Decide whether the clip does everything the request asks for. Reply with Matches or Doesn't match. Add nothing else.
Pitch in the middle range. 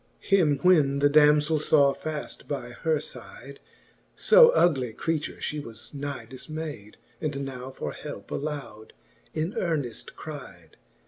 Matches